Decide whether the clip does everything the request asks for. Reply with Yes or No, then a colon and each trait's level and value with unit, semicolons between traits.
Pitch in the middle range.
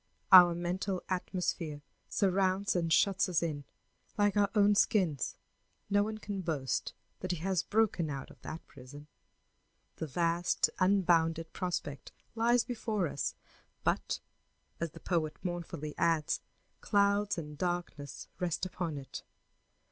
Yes: medium, 175 Hz